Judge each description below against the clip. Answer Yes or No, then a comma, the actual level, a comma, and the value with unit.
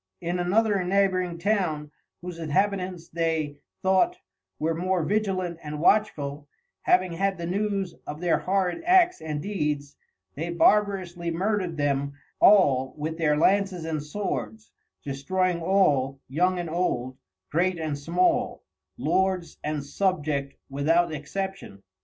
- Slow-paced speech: Yes, slow, 125 wpm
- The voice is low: No, medium, 170 Hz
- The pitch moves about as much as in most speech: Yes, average, 4.2 semitones